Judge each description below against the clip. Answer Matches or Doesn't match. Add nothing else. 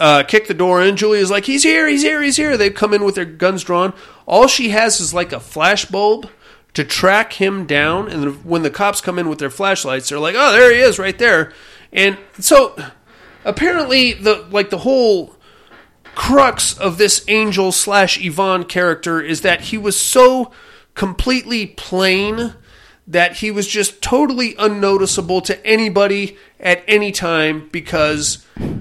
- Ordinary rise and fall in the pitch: Matches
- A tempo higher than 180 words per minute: Doesn't match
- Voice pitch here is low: Doesn't match